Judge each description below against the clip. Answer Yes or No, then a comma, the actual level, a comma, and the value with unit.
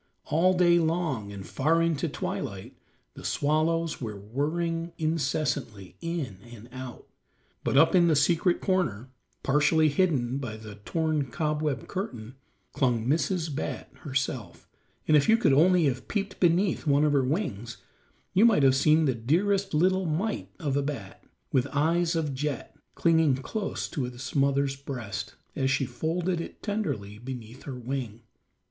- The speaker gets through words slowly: No, average, 155 wpm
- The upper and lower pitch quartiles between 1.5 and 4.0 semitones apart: No, average, 4.7 semitones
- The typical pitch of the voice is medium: Yes, medium, 145 Hz